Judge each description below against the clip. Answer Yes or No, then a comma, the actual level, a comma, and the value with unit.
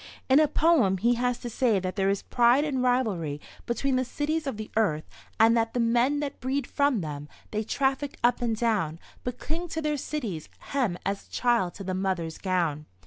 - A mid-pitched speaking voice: No, high, 235 Hz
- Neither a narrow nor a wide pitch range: No, wide, 5.9 semitones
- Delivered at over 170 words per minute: Yes, fast, 205 wpm